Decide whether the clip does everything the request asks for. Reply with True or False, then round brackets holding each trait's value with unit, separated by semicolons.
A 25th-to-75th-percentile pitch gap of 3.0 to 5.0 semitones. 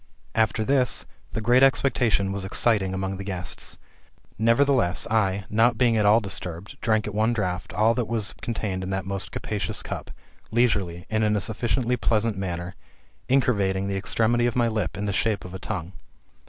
True (3.3 semitones)